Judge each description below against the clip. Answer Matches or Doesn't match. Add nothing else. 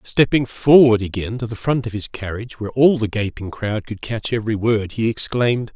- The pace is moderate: Doesn't match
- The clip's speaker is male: Matches